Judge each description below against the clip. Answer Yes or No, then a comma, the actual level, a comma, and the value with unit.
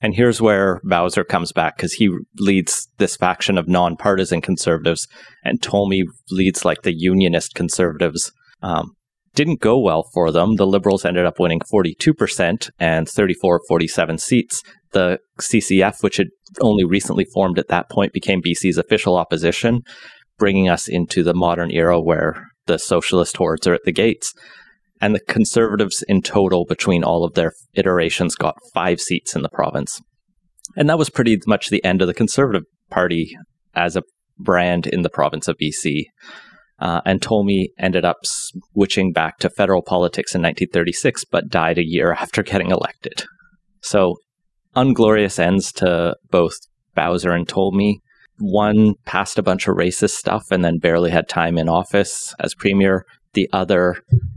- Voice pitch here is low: Yes, very low, 95 Hz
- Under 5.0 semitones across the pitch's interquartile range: Yes, average, 3.2 semitones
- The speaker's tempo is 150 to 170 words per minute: Yes, average, 160 wpm